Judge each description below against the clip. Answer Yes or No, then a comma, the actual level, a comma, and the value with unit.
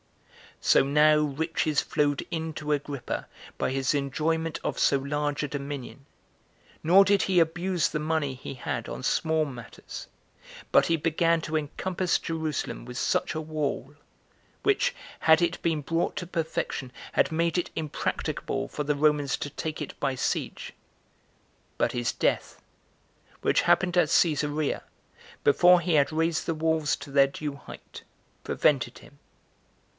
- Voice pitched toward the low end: No, medium, 155 Hz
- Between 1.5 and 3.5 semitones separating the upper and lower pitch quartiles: Yes, narrow, 2.5 semitones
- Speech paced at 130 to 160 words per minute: Yes, average, 150 wpm